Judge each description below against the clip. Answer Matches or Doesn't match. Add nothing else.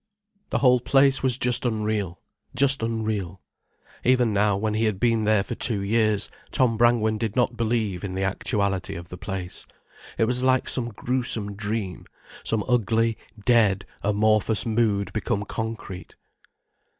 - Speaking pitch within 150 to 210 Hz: Doesn't match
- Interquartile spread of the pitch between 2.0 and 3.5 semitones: Matches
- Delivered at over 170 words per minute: Doesn't match